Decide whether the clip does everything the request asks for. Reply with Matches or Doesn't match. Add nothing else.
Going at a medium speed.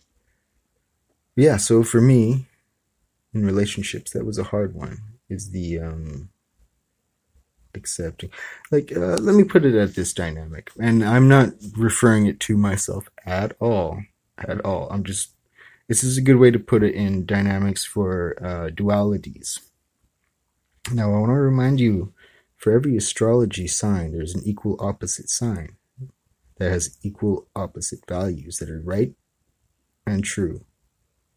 Matches